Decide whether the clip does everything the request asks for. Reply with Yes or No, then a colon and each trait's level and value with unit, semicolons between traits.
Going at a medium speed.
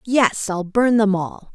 Yes: average, 195 wpm